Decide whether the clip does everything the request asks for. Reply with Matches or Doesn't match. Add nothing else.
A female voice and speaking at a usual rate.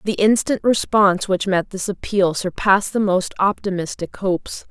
Matches